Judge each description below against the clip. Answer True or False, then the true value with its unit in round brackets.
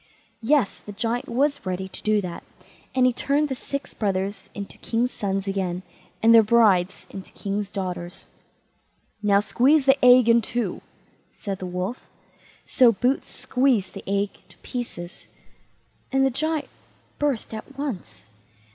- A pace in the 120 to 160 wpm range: True (145 wpm)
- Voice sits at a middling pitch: False (220 Hz)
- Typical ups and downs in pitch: True (4.7 semitones)